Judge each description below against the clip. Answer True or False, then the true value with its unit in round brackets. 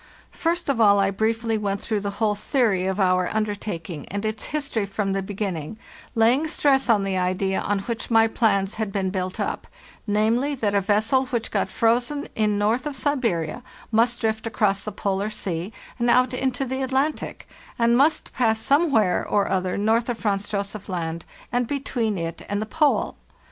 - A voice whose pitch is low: False (215 Hz)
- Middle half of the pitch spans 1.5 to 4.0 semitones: True (3.6 semitones)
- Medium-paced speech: True (180 wpm)